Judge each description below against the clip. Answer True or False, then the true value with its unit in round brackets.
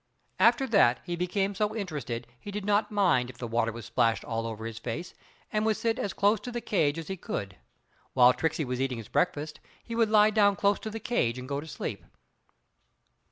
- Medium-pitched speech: True (170 Hz)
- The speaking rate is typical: False (220 wpm)